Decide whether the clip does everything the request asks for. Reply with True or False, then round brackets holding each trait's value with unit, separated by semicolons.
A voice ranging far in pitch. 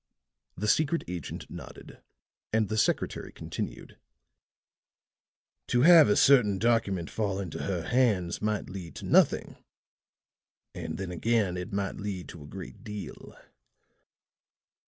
False (3.8 semitones)